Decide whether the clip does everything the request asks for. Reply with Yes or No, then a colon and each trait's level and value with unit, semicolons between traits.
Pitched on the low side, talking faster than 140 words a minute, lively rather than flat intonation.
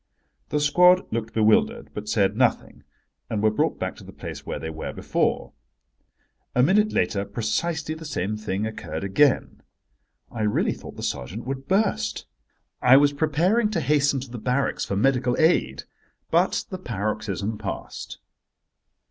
Yes: low, 125 Hz; average, 155 wpm; wide, 6.8 semitones